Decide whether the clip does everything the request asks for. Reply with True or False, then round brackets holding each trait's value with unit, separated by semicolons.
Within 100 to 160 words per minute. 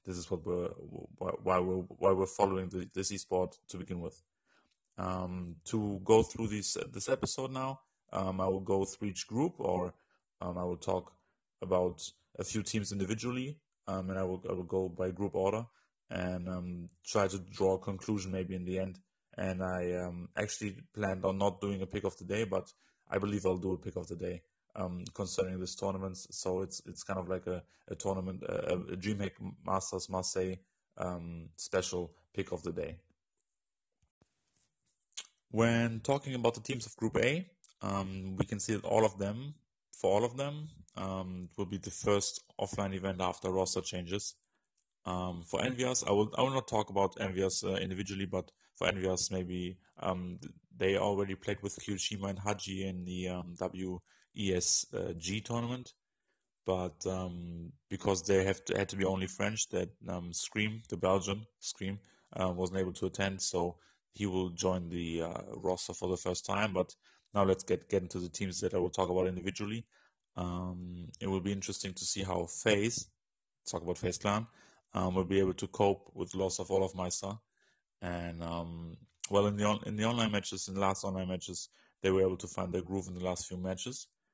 False (190 wpm)